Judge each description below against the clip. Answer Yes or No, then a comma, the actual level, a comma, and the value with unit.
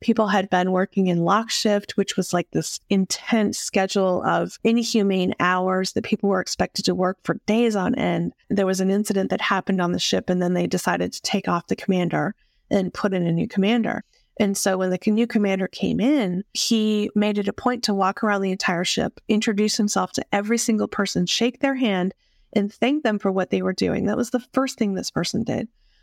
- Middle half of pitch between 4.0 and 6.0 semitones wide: No, average, 3.1 semitones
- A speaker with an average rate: No, fast, 215 wpm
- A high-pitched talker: Yes, high, 200 Hz